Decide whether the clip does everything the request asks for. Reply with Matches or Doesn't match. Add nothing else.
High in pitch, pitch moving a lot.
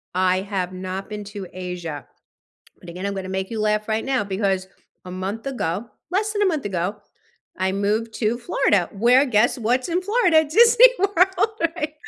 Matches